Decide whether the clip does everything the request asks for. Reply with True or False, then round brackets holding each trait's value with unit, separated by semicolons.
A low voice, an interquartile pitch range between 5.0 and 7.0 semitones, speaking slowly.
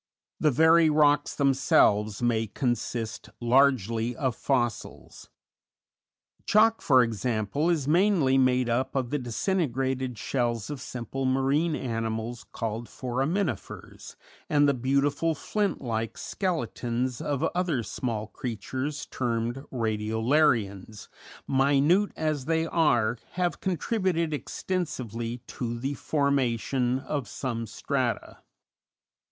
False (130 Hz; 4.2 semitones; 105 wpm)